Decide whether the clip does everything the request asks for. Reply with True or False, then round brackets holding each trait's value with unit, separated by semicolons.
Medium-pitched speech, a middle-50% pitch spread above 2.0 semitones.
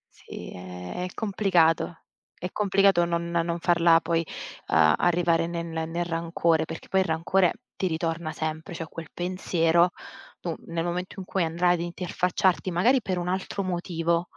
False (170 Hz; 1.6 semitones)